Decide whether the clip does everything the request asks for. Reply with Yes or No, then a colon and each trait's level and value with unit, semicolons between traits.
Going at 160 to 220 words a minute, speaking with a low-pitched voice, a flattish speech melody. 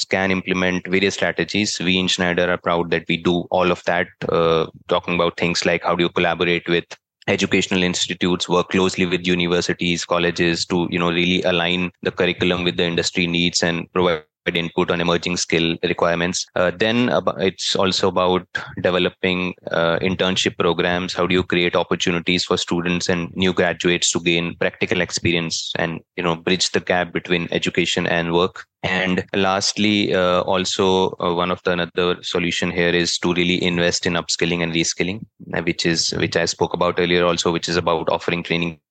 Yes: average, 180 wpm; very low, 90 Hz; narrow, 1.2 semitones